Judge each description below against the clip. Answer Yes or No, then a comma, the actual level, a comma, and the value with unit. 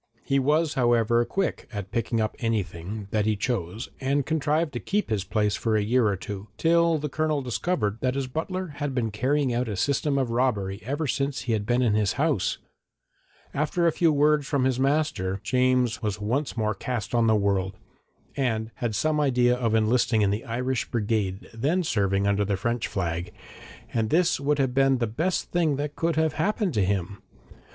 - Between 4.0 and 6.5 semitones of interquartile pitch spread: Yes, average, 5.3 semitones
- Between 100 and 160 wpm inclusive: No, average, 195 wpm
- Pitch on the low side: Yes, low, 120 Hz